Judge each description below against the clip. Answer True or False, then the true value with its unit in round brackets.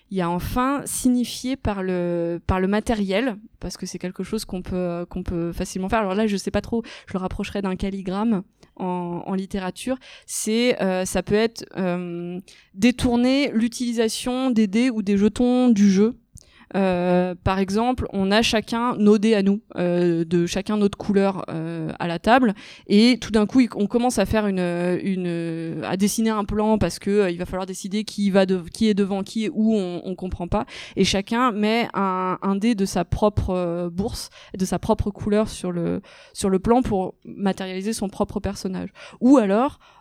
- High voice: True (200 Hz)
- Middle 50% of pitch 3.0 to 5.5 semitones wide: True (3.3 semitones)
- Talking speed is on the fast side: False (195 wpm)